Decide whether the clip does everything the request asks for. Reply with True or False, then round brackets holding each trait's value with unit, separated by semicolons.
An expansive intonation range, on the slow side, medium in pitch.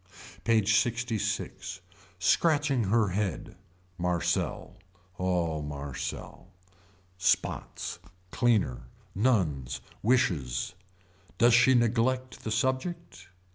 False (5.8 semitones; 75 wpm; 110 Hz)